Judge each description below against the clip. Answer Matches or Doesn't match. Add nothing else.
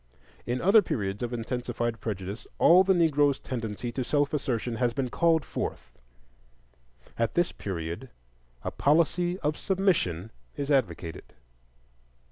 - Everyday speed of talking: Doesn't match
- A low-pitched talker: Matches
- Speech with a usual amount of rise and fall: Doesn't match